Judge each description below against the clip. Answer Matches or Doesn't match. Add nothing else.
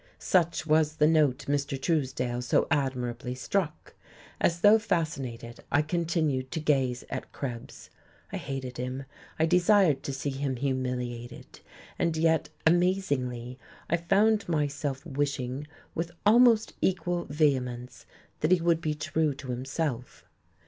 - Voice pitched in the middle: Matches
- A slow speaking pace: Matches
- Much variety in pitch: Doesn't match